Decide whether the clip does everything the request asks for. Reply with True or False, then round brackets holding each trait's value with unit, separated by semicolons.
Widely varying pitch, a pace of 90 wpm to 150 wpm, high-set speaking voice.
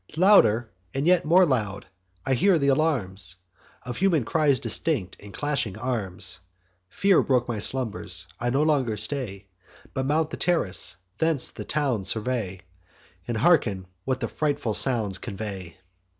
False (6.5 semitones; 145 wpm; 125 Hz)